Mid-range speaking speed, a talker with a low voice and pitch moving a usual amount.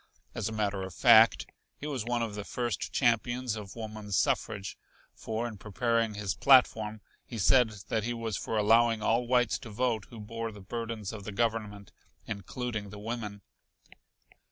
No: average, 170 wpm; low, 110 Hz; narrow, 2.2 semitones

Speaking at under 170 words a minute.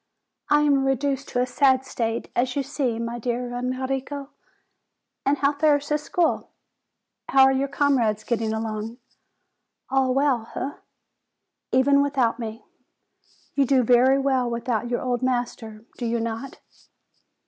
Yes: average, 140 wpm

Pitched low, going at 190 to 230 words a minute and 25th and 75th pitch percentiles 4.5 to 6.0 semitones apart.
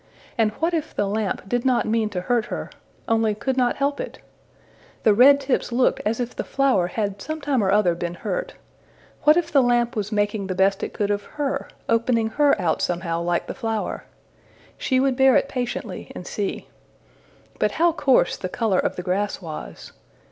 No: high, 225 Hz; average, 195 wpm; average, 5.0 semitones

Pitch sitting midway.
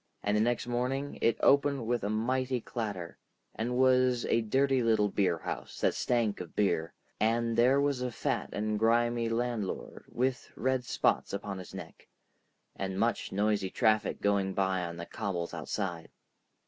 No: low, 115 Hz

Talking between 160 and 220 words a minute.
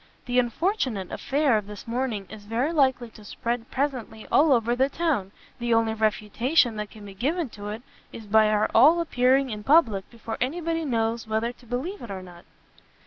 Yes: average, 195 wpm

